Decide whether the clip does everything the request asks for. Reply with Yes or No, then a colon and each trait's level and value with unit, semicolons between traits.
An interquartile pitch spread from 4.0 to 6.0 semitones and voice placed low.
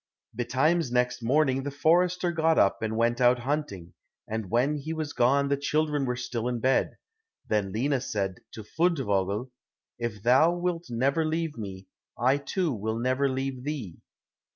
Yes: average, 4.6 semitones; low, 130 Hz